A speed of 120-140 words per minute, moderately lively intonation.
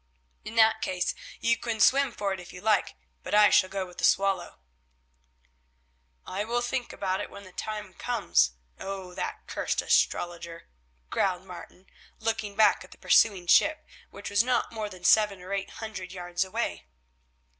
No: average, 170 wpm; average, 3.2 semitones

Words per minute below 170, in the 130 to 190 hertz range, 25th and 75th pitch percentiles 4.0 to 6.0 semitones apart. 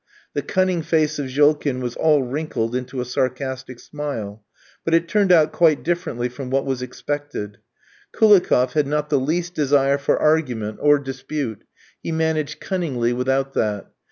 No: average, 155 wpm; medium, 140 Hz; average, 3.6 semitones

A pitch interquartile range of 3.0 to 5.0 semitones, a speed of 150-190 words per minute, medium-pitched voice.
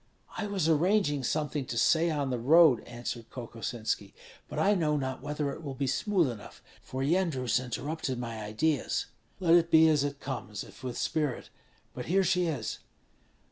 Yes: average, 4.7 semitones; average, 175 wpm; medium, 145 Hz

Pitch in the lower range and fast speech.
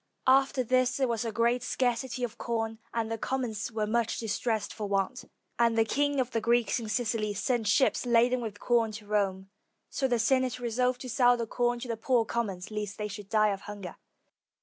No: high, 230 Hz; fast, 210 wpm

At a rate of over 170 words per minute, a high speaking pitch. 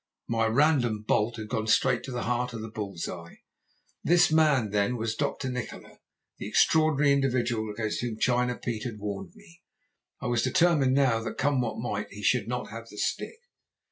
No: average, 185 wpm; low, 120 Hz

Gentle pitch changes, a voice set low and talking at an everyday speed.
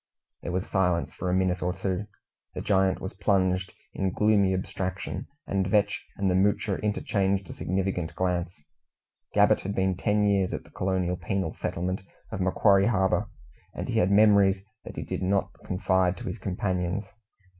Yes: narrow, 1.3 semitones; very low, 95 Hz; average, 165 wpm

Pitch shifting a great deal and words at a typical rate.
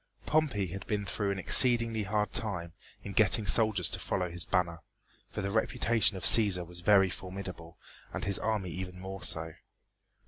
No: average, 3.0 semitones; average, 170 wpm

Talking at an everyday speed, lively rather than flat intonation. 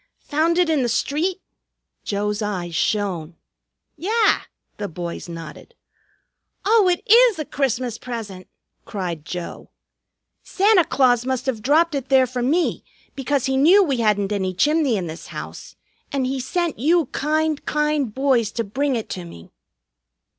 Yes: average, 150 wpm; wide, 7.0 semitones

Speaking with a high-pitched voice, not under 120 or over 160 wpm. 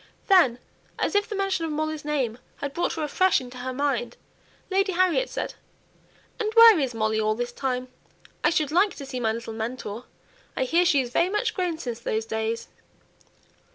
No: very high, 280 Hz; average, 190 wpm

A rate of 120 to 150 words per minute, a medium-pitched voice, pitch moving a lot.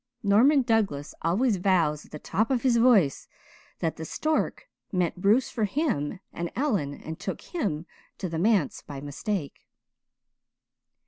No: average, 145 wpm; high, 195 Hz; wide, 6.8 semitones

